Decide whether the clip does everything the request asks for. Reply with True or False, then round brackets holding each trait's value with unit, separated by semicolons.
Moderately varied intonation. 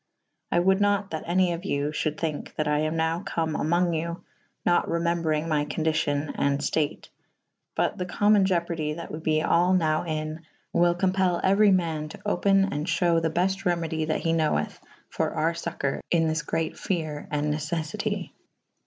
False (2.2 semitones)